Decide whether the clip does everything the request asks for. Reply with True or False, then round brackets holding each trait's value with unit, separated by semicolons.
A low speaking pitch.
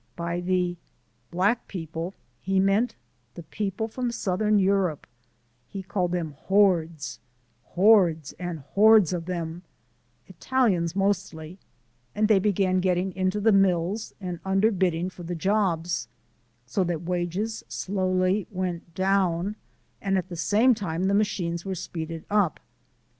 False (185 Hz)